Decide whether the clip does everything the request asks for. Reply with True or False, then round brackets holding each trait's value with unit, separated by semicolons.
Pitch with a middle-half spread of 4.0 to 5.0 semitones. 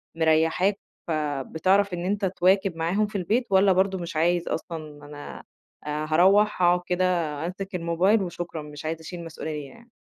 False (3.3 semitones)